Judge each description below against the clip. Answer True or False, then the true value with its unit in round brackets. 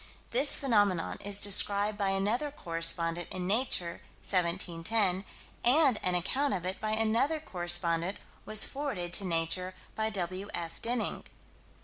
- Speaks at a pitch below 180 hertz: False (195 Hz)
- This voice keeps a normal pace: False (130 wpm)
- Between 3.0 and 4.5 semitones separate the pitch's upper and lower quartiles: True (4.1 semitones)